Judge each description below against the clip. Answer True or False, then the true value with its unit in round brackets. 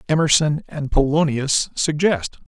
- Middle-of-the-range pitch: True (150 Hz)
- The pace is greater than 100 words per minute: False (95 wpm)